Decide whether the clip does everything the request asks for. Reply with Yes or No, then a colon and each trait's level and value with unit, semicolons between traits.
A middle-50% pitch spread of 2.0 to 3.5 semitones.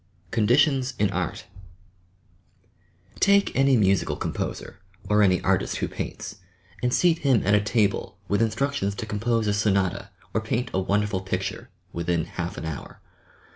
No: average, 4.0 semitones